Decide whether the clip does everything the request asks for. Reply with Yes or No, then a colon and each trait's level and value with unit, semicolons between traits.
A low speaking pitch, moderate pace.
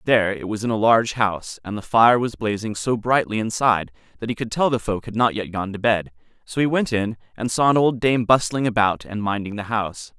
No: low, 110 Hz; fast, 245 wpm